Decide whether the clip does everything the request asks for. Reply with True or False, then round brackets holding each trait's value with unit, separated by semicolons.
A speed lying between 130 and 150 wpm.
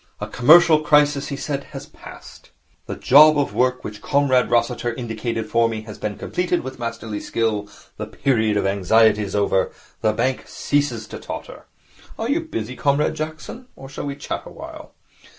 False (170 wpm)